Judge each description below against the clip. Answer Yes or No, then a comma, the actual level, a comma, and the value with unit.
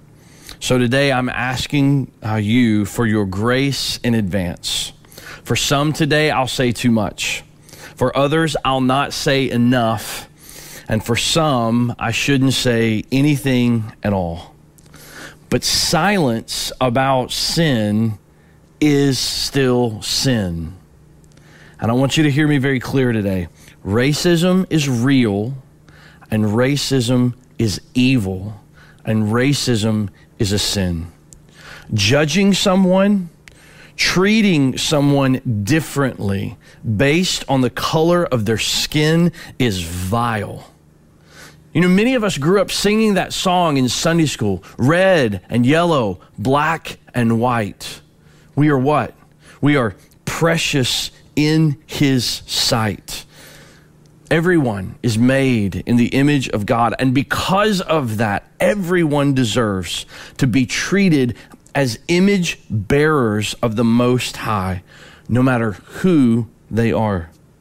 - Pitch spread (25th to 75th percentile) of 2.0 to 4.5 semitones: No, average, 5.3 semitones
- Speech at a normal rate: No, slow, 120 wpm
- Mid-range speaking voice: No, low, 125 Hz